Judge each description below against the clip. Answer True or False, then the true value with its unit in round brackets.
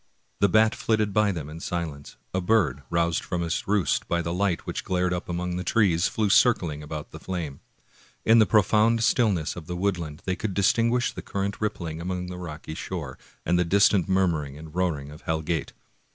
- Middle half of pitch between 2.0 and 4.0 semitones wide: True (3.7 semitones)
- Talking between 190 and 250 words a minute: True (195 wpm)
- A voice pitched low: True (90 Hz)